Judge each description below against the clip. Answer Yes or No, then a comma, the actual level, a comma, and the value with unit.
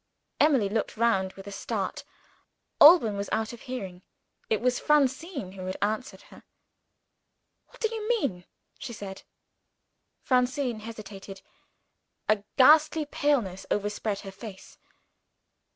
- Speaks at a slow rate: Yes, slow, 120 wpm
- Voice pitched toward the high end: Yes, high, 220 Hz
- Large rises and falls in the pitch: Yes, wide, 5.7 semitones